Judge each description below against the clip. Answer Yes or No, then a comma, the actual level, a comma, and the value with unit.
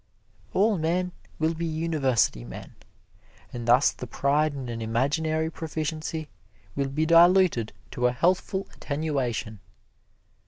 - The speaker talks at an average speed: No, slow, 120 wpm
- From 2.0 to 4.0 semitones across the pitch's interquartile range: No, average, 4.7 semitones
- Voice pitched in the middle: Yes, medium, 155 Hz